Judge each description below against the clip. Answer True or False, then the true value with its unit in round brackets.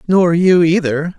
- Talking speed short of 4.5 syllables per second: True (4.0 syllables/s)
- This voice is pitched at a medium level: True (170 Hz)